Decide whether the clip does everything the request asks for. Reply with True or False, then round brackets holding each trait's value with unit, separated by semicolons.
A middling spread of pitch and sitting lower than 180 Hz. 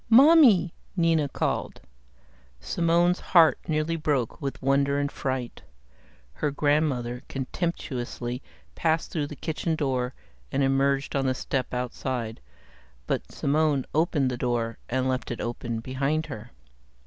True (3.8 semitones; 140 Hz)